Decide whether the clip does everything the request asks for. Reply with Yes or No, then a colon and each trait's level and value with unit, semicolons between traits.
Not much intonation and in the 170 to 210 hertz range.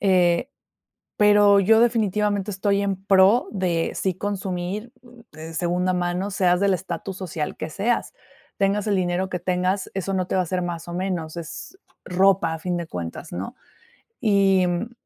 Yes: narrow, 2.2 semitones; medium, 185 Hz